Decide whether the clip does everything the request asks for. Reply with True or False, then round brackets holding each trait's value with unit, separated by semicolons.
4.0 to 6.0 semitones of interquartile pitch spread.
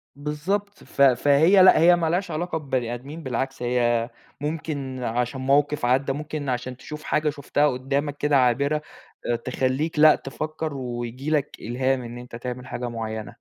False (3.5 semitones)